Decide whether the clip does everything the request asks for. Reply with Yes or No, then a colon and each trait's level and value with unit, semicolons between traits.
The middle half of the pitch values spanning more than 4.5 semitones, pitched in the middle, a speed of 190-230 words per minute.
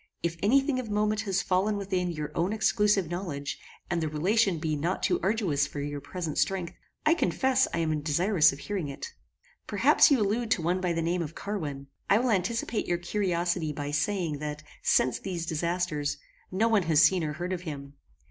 Yes: average, 5.0 semitones; medium, 175 Hz; average, 195 wpm